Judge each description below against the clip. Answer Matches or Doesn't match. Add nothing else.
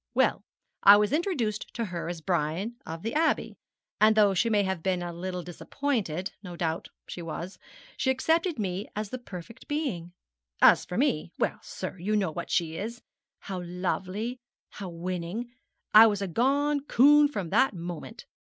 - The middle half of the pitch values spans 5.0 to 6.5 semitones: Matches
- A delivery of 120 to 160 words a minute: Doesn't match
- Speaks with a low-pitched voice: Doesn't match